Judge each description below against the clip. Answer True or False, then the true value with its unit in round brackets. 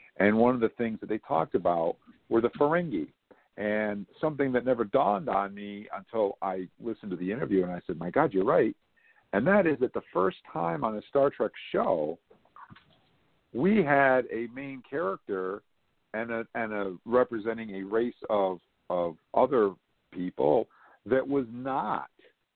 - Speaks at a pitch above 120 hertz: False (110 Hz)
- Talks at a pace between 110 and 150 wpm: False (170 wpm)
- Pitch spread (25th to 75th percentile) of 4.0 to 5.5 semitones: True (4.4 semitones)